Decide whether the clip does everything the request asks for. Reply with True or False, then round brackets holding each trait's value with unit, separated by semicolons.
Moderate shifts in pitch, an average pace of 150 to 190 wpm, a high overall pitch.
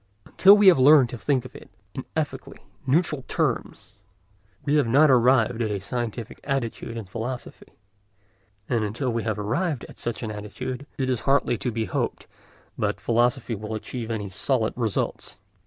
False (3.2 semitones; 170 wpm; 120 Hz)